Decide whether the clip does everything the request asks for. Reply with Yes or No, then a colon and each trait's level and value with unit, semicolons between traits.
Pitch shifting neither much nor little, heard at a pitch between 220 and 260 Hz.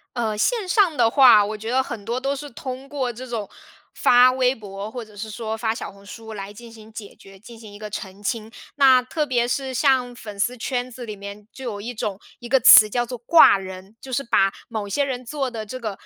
Yes: average, 3.4 semitones; high, 230 Hz